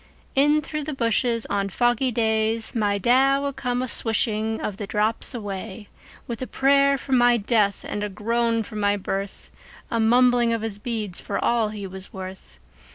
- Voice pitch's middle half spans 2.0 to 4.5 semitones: Yes, average, 3.0 semitones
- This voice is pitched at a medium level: No, high, 225 Hz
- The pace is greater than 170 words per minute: Yes, average, 180 wpm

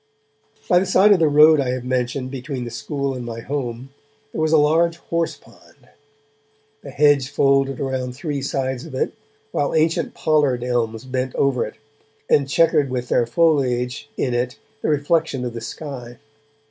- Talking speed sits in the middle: Yes, average, 170 wpm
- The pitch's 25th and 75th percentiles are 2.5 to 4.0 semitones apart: Yes, average, 3.2 semitones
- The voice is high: No, low, 135 Hz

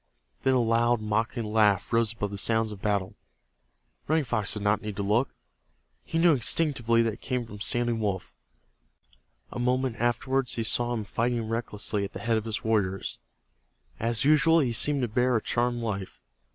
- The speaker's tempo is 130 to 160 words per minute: No, average, 180 wpm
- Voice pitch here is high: No, low, 115 Hz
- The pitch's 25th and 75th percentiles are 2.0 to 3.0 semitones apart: Yes, narrow, 2.5 semitones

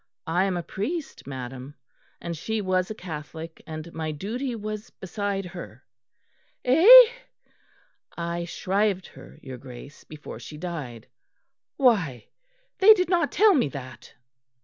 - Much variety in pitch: Yes, wide, 6.4 semitones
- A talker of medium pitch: Yes, medium, 180 Hz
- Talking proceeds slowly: Yes, slow, 130 wpm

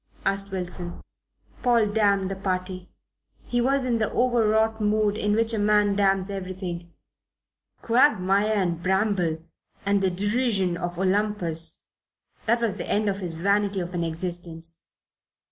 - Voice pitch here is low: No, high, 195 Hz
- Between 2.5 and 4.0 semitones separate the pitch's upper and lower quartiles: Yes, average, 2.8 semitones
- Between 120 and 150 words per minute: Yes, average, 140 wpm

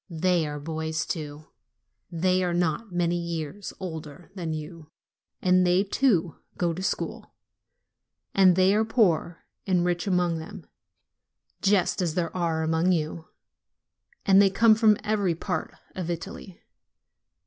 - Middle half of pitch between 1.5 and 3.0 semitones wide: Yes, average, 2.7 semitones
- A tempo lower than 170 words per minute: Yes, slow, 135 wpm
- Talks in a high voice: No, medium, 175 Hz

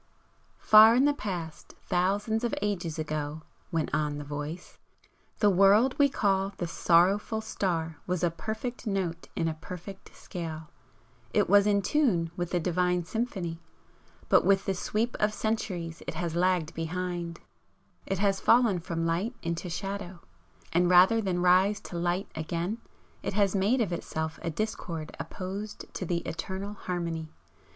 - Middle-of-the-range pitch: Yes, medium, 180 Hz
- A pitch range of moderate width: Yes, average, 3.5 semitones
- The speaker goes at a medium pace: Yes, average, 155 wpm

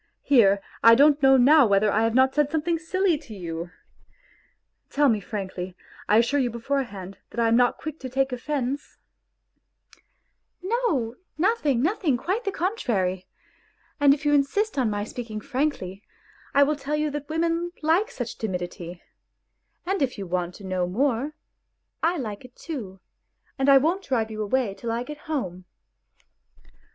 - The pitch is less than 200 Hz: No, very high, 260 Hz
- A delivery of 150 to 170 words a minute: Yes, average, 165 wpm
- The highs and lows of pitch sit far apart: Yes, wide, 6.0 semitones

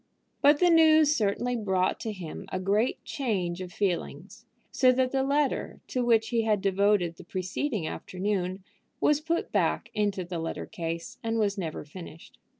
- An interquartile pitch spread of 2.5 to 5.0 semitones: No, wide, 5.6 semitones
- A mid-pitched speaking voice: No, high, 205 Hz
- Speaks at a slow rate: No, average, 165 wpm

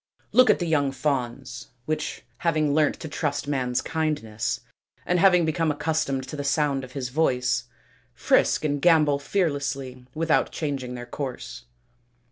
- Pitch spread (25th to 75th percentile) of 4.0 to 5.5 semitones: No, average, 3.3 semitones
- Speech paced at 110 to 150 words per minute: Yes, average, 145 wpm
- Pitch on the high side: No, medium, 145 Hz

